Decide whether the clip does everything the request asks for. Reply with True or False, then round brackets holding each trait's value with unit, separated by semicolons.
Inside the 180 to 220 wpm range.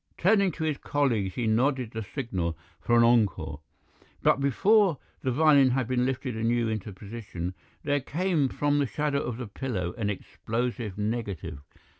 False (160 wpm)